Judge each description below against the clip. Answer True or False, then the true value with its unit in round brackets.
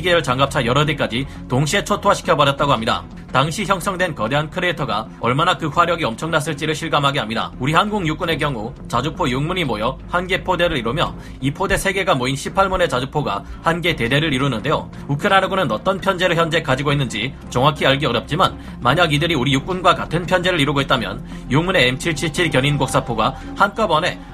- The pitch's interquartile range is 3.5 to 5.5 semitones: True (5.1 semitones)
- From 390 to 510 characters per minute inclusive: True (415 characters per minute)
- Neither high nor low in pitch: True (155 Hz)